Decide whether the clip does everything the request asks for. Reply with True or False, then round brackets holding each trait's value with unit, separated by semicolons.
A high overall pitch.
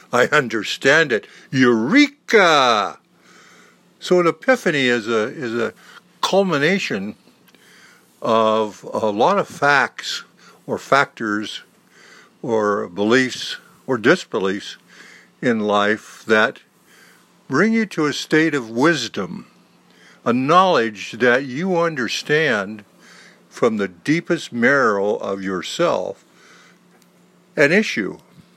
False (125 Hz)